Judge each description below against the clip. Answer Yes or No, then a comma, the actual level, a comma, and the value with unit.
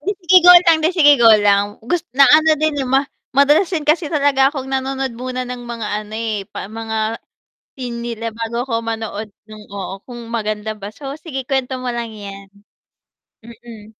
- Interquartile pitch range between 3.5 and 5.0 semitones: Yes, average, 4.0 semitones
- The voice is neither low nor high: No, high, 240 Hz